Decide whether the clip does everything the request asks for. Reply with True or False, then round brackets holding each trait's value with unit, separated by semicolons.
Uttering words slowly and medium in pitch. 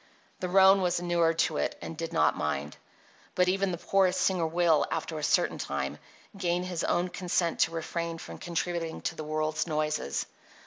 False (180 wpm; 170 Hz)